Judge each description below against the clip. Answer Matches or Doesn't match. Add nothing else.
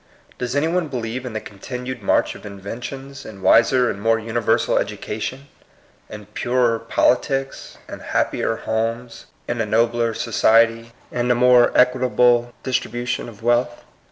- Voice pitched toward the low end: Matches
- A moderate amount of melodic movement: Doesn't match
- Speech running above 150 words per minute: Doesn't match